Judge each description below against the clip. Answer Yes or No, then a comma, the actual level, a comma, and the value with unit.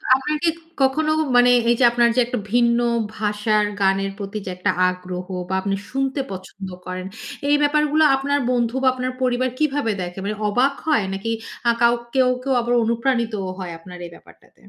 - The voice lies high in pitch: Yes, high, 235 Hz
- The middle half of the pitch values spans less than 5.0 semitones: No, average, 5.3 semitones